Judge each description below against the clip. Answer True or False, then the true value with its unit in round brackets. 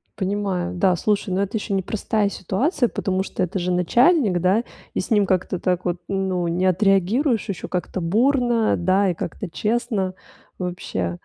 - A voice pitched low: False (190 Hz)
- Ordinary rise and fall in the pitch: True (3.1 semitones)